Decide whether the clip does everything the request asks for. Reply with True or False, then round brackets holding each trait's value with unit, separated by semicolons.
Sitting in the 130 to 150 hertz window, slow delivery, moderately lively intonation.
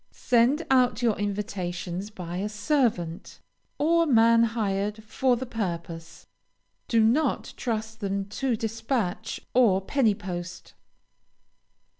False (220 Hz; 110 wpm; 3.8 semitones)